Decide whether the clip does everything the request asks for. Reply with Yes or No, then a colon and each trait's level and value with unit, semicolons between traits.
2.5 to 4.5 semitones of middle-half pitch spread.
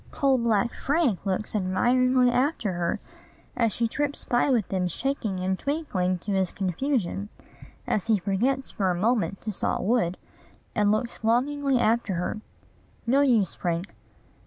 No: average, 5.1 semitones